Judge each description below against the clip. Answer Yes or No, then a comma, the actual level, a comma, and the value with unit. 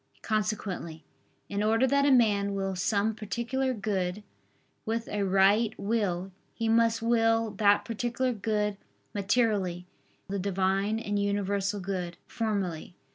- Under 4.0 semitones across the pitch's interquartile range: Yes, average, 2.7 semitones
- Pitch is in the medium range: No, high, 205 Hz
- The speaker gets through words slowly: Yes, slow, 130 wpm